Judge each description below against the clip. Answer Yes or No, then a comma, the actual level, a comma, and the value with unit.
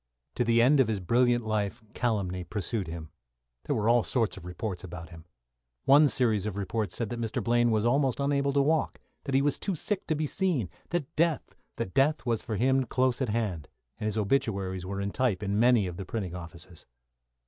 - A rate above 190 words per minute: Yes, fast, 205 wpm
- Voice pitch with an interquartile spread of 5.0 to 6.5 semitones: Yes, average, 5.3 semitones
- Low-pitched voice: Yes, low, 115 Hz